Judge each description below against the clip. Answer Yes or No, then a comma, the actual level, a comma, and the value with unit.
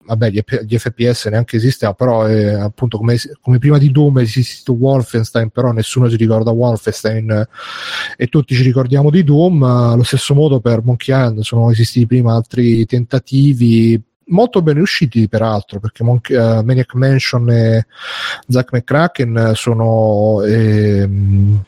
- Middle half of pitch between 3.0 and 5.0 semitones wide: No, narrow, 2.5 semitones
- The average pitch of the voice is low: Yes, low, 120 Hz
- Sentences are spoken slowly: No, average, 155 wpm